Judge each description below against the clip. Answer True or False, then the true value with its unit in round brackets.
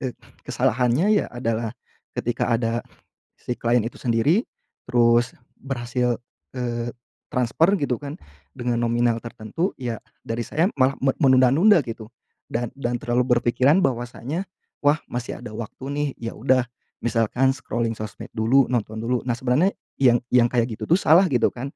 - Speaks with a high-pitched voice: False (120 Hz)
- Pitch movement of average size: False (2.3 semitones)